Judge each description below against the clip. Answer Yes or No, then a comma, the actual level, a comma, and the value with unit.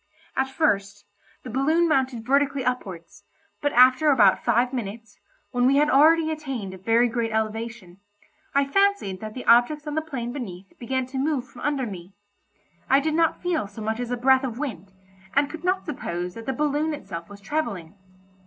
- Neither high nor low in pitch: No, very high, 255 Hz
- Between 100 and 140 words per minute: No, average, 185 wpm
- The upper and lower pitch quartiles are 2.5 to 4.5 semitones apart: No, average, 5.2 semitones